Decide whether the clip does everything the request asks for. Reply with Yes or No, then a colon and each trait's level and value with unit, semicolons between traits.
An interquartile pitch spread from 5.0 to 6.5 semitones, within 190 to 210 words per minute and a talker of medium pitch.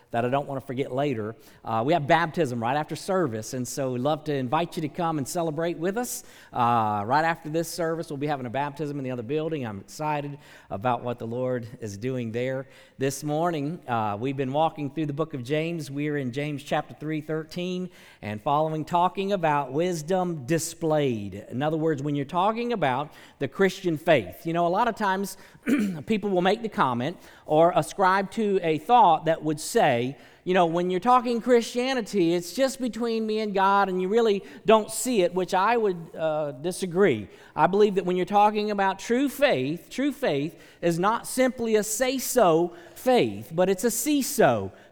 Yes: wide, 5.4 semitones; average, 200 wpm; medium, 165 Hz